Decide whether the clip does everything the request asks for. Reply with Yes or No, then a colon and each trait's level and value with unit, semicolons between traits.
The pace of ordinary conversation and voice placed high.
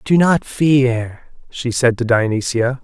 No: average, 150 wpm; low, 125 Hz